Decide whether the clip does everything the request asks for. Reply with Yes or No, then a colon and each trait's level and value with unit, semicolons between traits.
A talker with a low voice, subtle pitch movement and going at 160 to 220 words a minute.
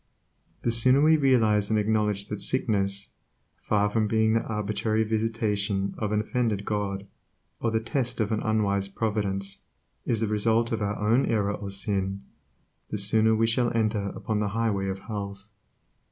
Yes: low, 105 Hz; narrow, 1.9 semitones; average, 165 wpm